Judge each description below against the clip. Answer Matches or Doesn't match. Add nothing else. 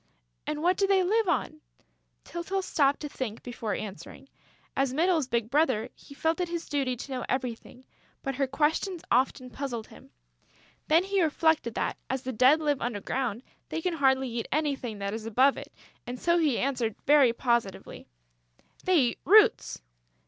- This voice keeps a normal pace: Matches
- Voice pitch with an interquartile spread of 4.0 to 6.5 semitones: Matches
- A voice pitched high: Matches